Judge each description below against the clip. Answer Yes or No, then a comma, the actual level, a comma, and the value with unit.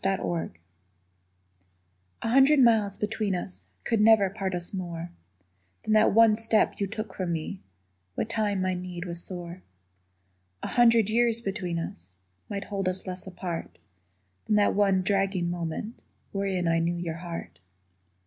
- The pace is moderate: Yes, average, 150 wpm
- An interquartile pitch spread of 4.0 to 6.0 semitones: No, average, 3.5 semitones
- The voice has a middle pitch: No, high, 195 Hz